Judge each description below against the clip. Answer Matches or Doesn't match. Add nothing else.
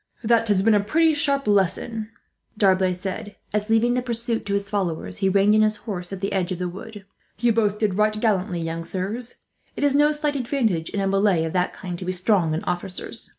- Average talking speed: Doesn't match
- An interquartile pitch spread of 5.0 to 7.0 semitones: Doesn't match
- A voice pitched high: Matches